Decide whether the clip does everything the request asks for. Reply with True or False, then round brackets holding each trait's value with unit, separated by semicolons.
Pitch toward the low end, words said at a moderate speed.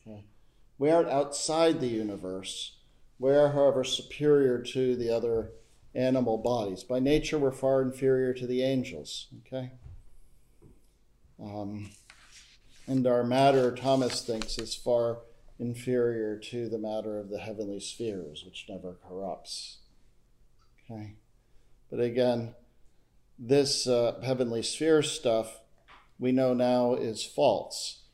False (120 Hz; 115 wpm)